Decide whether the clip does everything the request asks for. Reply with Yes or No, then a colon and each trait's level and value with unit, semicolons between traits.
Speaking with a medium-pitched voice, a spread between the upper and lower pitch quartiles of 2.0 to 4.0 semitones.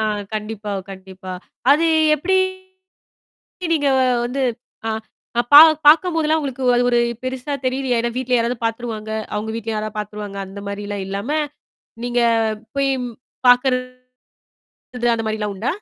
No: high, 240 Hz; average, 3.5 semitones